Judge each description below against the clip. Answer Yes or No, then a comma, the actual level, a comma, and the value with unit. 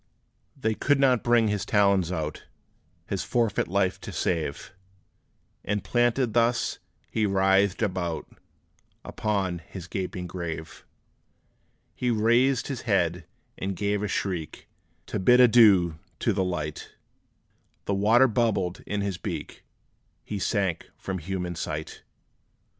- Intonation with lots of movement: No, average, 3.9 semitones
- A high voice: No, low, 100 Hz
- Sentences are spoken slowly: Yes, slow, 120 wpm